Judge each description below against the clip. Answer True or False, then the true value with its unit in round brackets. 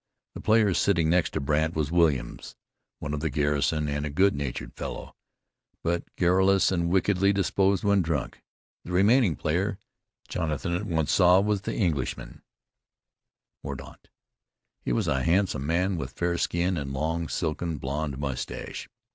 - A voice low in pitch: True (85 Hz)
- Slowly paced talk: False (150 wpm)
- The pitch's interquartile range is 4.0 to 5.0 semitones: True (4.3 semitones)